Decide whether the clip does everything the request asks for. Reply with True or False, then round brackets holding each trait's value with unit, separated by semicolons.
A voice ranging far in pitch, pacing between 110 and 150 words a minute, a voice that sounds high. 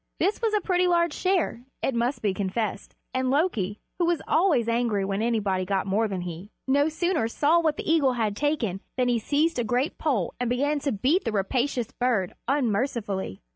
False (6.5 semitones; 195 wpm; 245 Hz)